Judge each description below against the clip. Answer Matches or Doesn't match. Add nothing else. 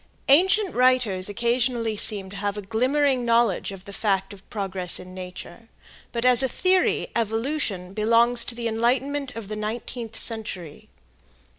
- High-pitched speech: Matches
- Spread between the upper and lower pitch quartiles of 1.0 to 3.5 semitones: Doesn't match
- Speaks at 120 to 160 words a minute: Matches